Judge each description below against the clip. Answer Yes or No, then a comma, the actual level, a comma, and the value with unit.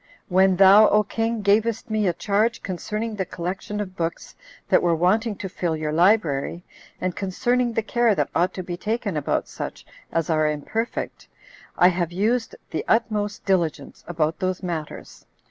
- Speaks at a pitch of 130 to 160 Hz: No, high, 190 Hz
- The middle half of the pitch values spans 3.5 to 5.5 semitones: Yes, average, 3.9 semitones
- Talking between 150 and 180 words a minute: Yes, average, 165 wpm